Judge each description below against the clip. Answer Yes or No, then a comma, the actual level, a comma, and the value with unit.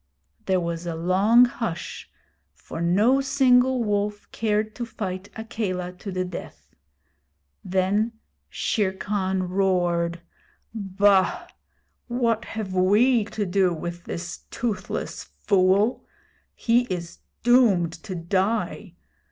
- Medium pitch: No, high, 195 Hz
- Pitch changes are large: No, average, 3.8 semitones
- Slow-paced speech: Yes, slow, 110 wpm